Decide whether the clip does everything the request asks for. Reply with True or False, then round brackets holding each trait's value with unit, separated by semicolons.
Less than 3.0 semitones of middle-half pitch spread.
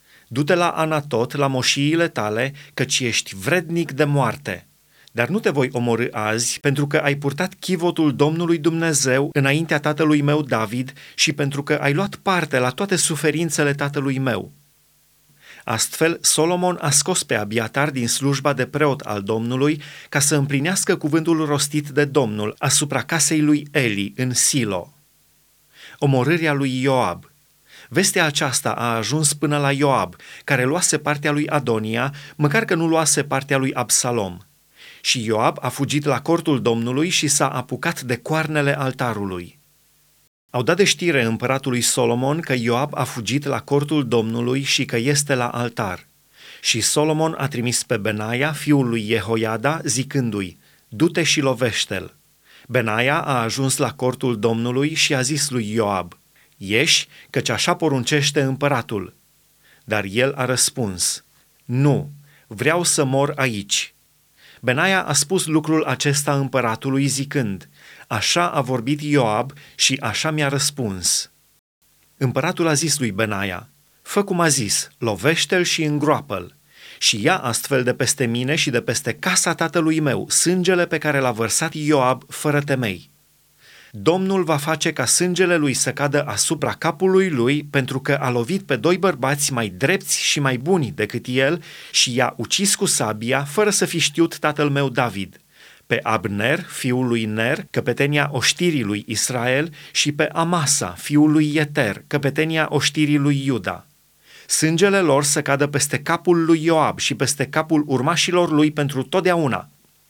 False (3.8 semitones)